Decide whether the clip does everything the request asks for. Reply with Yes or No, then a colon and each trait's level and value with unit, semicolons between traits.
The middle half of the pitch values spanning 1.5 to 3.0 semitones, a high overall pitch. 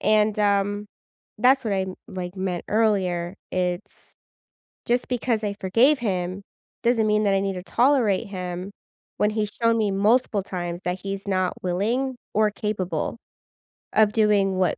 Yes: average, 2.7 semitones; high, 200 Hz